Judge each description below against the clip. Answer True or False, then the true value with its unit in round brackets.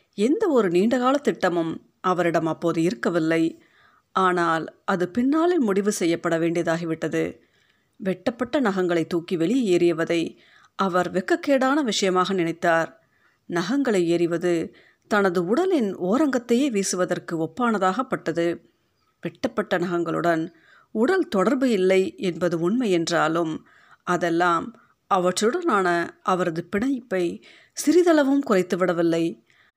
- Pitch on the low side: False (185 Hz)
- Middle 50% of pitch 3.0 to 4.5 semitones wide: False (5.3 semitones)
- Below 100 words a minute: True (85 wpm)